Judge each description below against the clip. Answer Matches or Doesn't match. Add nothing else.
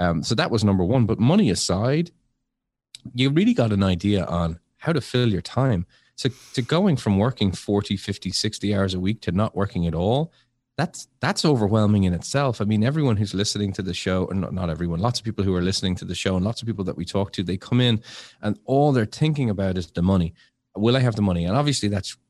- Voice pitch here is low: Matches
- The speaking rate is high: Matches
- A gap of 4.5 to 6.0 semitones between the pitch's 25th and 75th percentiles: Matches